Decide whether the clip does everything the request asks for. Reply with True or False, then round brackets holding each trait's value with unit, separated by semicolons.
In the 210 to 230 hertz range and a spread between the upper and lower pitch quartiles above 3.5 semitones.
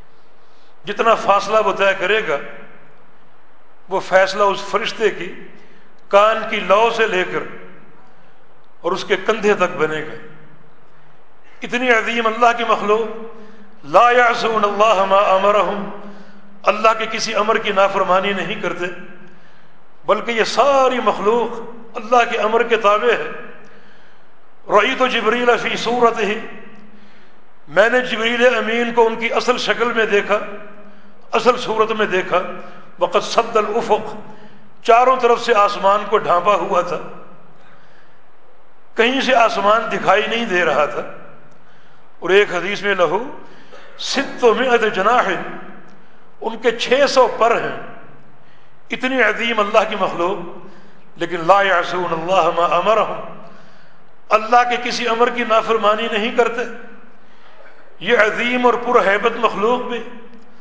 False (215 Hz; 2.9 semitones)